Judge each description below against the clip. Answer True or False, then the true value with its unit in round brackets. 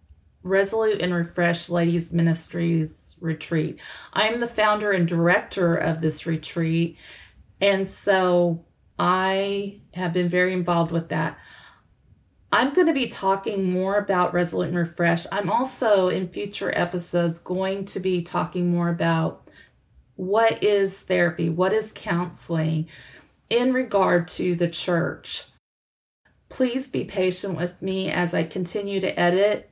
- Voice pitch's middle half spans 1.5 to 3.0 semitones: True (2.5 semitones)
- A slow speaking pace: True (130 wpm)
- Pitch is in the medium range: True (180 Hz)